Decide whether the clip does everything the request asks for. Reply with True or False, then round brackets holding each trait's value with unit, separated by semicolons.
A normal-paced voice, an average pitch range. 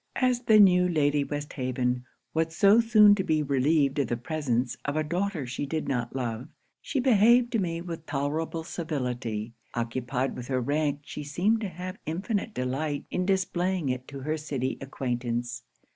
False (170 wpm; 6.0 semitones)